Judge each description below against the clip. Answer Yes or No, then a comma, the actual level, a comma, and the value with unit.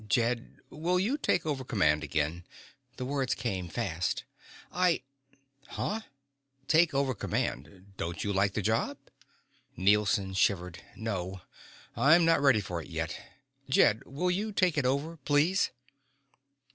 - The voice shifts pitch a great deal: Yes, wide, 8.2 semitones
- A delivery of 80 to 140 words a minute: Yes, slow, 135 wpm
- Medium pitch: No, low, 120 Hz